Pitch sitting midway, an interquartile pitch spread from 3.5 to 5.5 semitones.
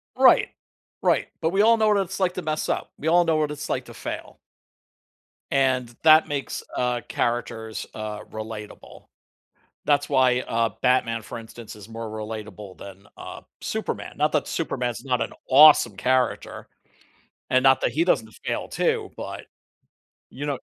No: low, 125 Hz; average, 4.9 semitones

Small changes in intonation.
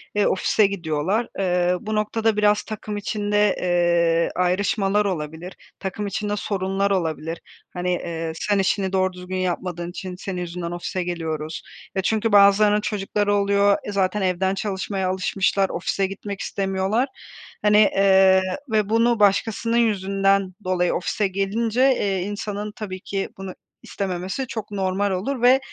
Yes: narrow, 2.2 semitones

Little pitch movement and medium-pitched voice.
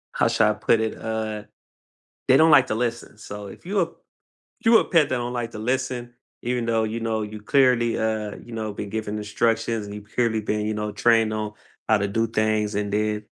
No: narrow, 2.1 semitones; low, 110 Hz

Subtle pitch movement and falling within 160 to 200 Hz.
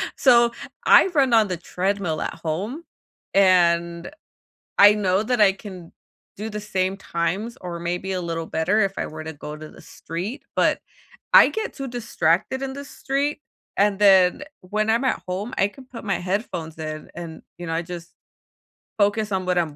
No: average, 4.3 semitones; high, 190 Hz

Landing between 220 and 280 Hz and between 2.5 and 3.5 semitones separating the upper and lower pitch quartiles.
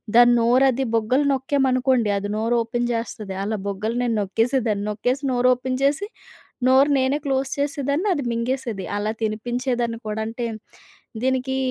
Yes: high, 245 Hz; average, 2.8 semitones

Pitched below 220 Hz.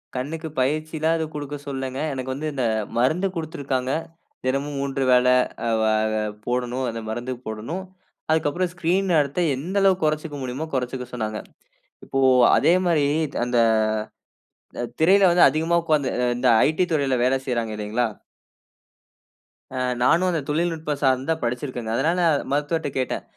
Yes: medium, 140 Hz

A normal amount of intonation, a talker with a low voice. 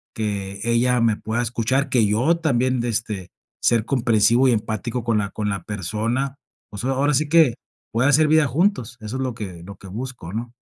Yes: average, 3.5 semitones; low, 115 Hz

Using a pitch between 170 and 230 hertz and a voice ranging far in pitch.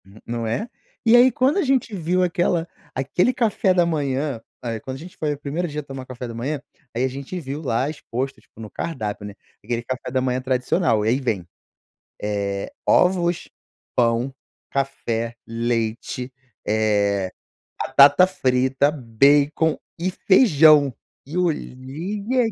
No: low, 135 Hz; wide, 6.1 semitones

